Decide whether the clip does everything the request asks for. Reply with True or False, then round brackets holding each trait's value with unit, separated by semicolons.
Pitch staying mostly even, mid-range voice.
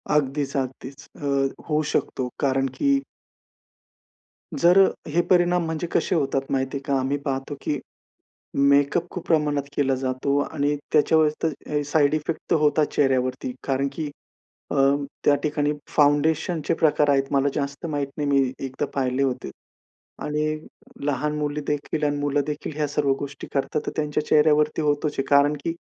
True (1.7 semitones; 145 Hz)